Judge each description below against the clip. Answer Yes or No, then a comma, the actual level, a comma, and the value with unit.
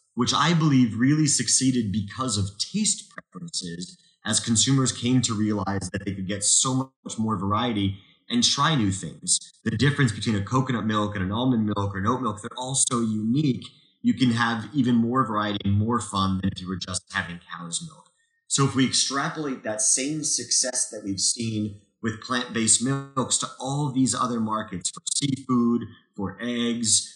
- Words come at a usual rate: Yes, average, 190 wpm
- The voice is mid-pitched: No, low, 115 Hz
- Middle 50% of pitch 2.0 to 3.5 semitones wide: No, average, 4.3 semitones